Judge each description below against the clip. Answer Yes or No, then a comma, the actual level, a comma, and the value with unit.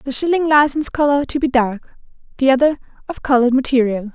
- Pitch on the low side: No, very high, 265 Hz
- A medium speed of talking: Yes, average, 175 wpm